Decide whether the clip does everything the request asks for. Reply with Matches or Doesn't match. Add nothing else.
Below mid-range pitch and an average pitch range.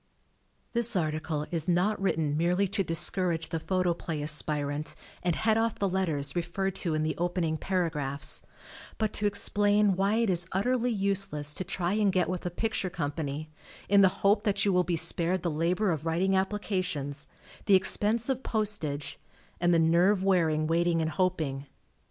Doesn't match